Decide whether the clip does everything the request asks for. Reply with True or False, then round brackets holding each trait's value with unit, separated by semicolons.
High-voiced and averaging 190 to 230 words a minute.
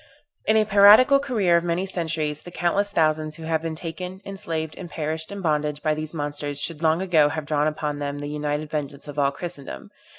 False (160 Hz; 205 wpm)